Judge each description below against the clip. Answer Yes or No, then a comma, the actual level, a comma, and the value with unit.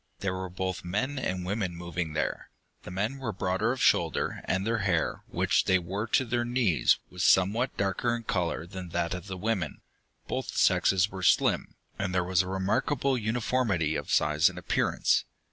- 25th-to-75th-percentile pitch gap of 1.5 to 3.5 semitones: No, average, 4.0 semitones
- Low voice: Yes, very low, 95 Hz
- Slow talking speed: No, average, 180 wpm